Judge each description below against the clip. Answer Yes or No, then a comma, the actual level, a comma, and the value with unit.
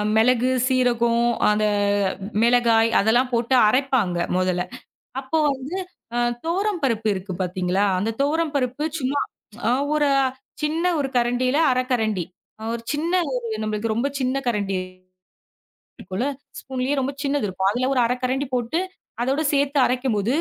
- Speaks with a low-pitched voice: No, very high, 250 Hz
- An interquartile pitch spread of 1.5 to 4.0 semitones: Yes, average, 3.7 semitones